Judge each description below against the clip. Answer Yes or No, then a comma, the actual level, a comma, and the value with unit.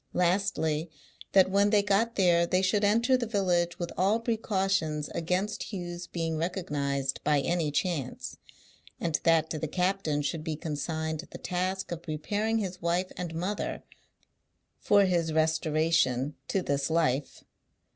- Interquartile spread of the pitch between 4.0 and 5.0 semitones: No, average, 3.6 semitones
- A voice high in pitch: No, medium, 175 Hz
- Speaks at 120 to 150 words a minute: Yes, average, 145 wpm